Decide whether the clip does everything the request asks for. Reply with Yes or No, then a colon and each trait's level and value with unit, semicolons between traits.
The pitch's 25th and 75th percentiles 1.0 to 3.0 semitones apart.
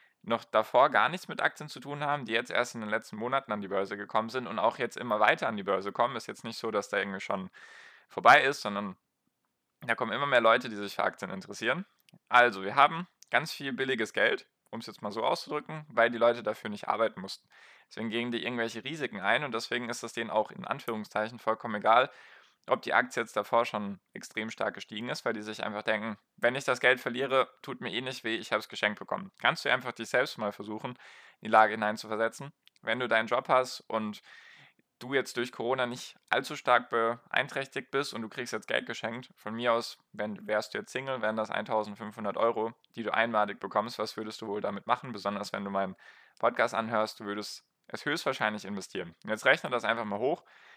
Yes: narrow, 2.4 semitones